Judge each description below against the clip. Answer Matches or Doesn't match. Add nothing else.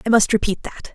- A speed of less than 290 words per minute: Matches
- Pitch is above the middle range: Matches